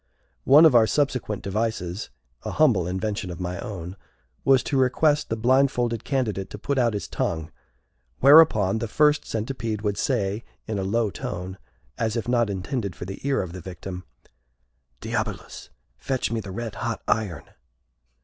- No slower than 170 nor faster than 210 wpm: No, average, 160 wpm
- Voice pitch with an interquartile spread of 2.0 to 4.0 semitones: No, average, 5.0 semitones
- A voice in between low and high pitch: No, low, 110 Hz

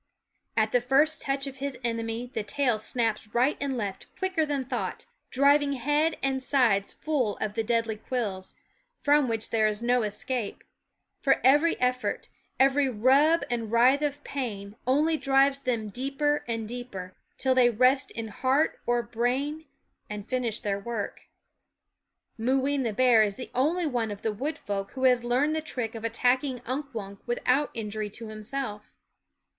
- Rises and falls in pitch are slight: No, average, 3.8 semitones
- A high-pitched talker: Yes, very high, 250 Hz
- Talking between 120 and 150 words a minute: No, average, 165 wpm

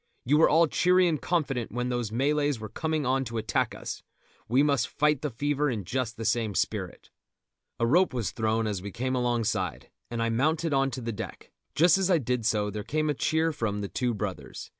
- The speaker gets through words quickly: Yes, fast, 215 wpm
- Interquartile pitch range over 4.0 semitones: Yes, average, 5.0 semitones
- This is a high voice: No, low, 125 Hz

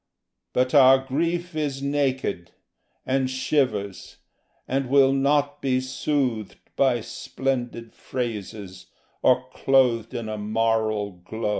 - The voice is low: Yes, low, 130 Hz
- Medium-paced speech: No, slow, 110 wpm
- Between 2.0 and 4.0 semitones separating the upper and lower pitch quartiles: Yes, average, 3.6 semitones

